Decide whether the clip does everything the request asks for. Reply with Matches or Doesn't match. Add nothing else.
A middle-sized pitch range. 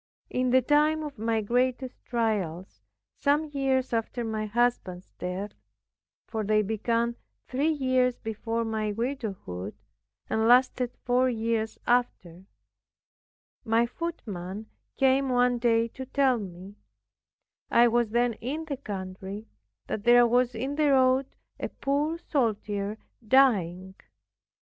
Matches